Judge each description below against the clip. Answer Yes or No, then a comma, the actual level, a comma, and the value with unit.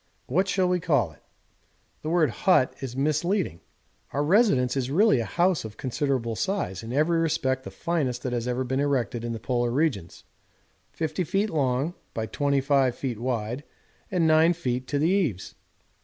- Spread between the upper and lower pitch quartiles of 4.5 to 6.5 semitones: Yes, average, 5.1 semitones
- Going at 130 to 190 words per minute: Yes, average, 170 wpm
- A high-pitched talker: No, medium, 140 Hz